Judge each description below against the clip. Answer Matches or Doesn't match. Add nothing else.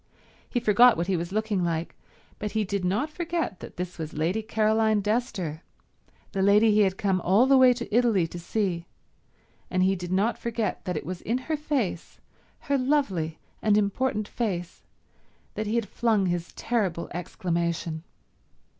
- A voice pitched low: Doesn't match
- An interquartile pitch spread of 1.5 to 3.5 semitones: Doesn't match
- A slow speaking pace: Doesn't match